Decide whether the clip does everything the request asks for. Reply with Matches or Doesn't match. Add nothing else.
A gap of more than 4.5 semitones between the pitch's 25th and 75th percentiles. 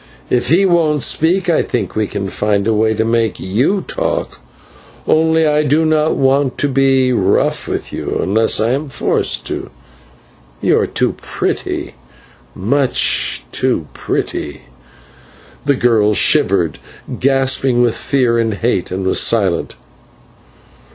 Matches